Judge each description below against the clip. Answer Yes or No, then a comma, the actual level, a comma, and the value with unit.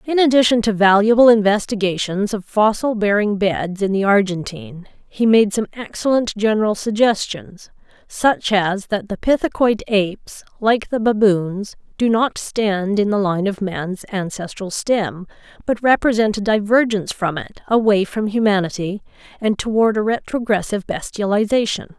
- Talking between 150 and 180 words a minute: No, average, 140 wpm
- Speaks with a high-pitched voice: Yes, high, 210 Hz